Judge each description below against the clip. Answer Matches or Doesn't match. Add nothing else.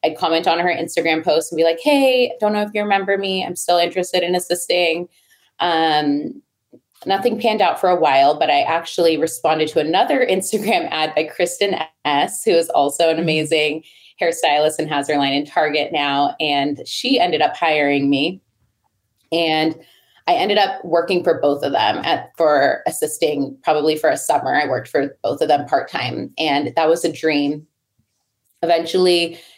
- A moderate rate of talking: Matches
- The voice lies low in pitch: Doesn't match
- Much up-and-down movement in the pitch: Doesn't match